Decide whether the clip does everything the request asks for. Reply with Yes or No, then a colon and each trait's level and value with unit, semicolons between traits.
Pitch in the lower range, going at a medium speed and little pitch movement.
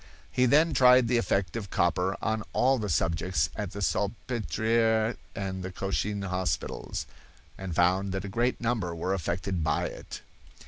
No: low, 100 Hz; average, 155 wpm; average, 3.8 semitones